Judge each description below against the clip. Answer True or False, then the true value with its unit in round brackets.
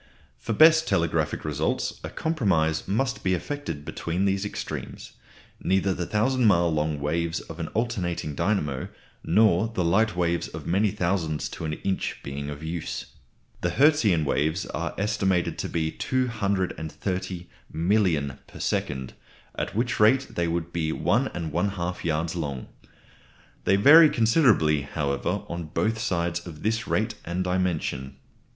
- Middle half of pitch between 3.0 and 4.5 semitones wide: False (5.0 semitones)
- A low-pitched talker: True (85 Hz)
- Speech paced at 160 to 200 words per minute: False (140 wpm)